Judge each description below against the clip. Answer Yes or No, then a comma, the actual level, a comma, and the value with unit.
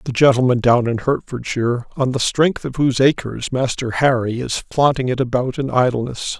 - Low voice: Yes, low, 125 Hz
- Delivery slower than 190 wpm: Yes, average, 180 wpm